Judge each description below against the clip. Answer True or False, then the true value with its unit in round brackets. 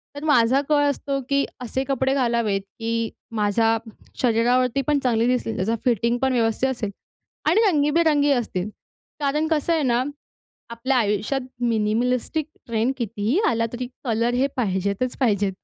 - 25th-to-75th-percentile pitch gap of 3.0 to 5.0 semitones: True (3.4 semitones)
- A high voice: True (245 Hz)